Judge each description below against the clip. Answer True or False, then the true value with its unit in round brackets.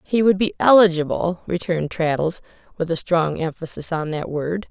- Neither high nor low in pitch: True (170 Hz)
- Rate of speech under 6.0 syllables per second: True (5.0 syllables/s)